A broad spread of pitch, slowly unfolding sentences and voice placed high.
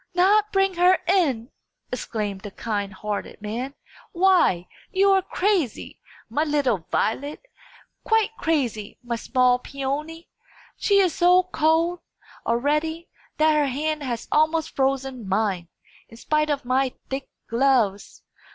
Yes: wide, 6.3 semitones; slow, 125 wpm; very high, 280 Hz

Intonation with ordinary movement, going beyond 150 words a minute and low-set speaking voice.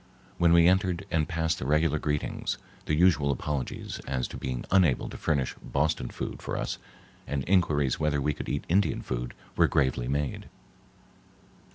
Yes: average, 3.5 semitones; average, 165 wpm; very low, 75 Hz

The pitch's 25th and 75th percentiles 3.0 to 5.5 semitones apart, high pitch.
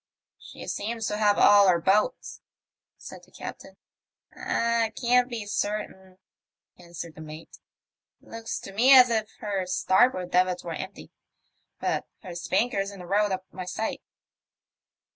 Yes: average, 3.6 semitones; high, 200 Hz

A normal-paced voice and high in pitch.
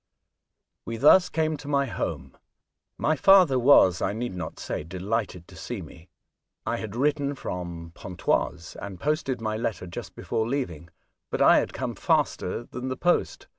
No: average, 165 wpm; low, 115 Hz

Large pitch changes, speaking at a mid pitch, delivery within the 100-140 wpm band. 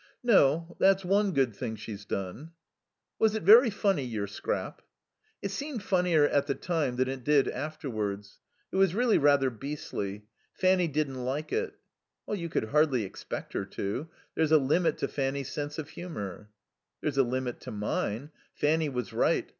No: wide, 6.1 semitones; medium, 145 Hz; average, 165 wpm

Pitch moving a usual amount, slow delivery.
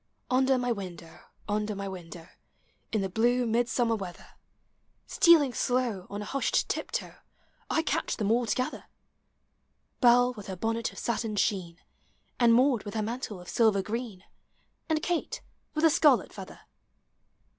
No: average, 3.9 semitones; average, 150 wpm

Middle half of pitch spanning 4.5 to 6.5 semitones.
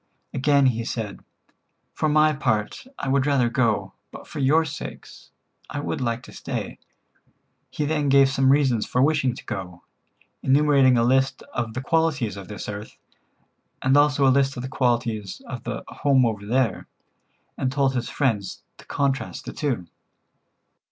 No: average, 3.3 semitones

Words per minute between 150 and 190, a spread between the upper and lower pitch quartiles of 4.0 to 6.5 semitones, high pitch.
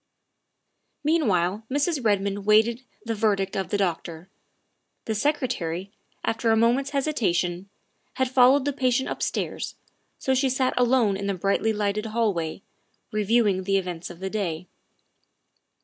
No: slow, 135 wpm; average, 4.7 semitones; high, 215 Hz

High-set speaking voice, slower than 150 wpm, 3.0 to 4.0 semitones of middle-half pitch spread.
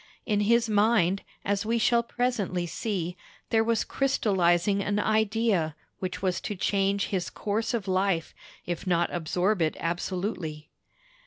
Yes: high, 200 Hz; average, 140 wpm; average, 3.7 semitones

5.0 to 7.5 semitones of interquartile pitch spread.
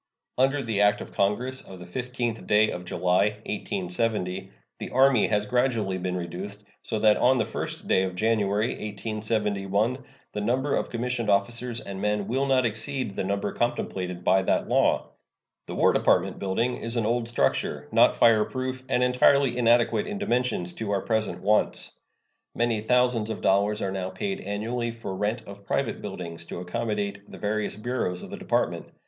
No: average, 3.5 semitones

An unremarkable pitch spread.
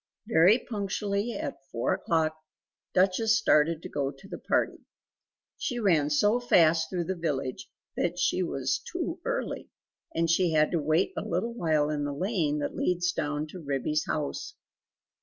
Yes: average, 4.6 semitones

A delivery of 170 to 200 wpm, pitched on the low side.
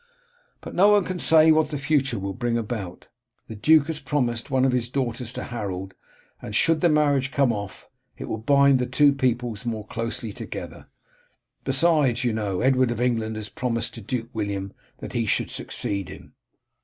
Yes: average, 185 wpm; low, 125 Hz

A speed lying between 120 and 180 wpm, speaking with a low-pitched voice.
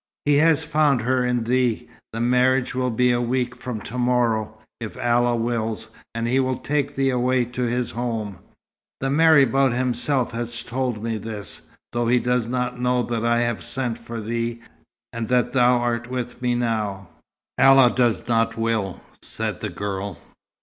Yes: average, 170 wpm; low, 120 Hz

